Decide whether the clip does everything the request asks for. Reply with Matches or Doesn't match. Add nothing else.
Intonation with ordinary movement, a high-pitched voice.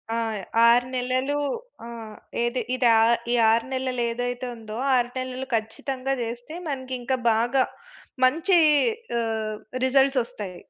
Doesn't match